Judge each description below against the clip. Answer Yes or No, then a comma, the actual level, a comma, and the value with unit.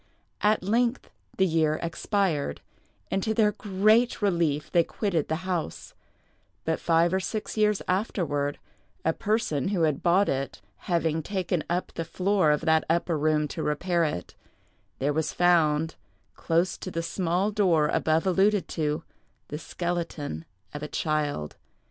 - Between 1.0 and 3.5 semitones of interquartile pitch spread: No, average, 3.9 semitones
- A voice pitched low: No, medium, 170 Hz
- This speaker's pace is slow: No, average, 150 wpm